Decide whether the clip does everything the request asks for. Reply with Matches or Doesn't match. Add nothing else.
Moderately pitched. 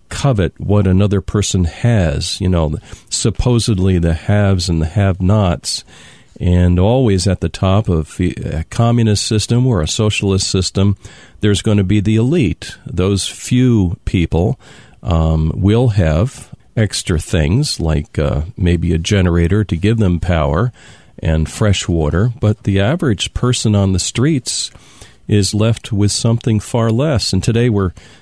Doesn't match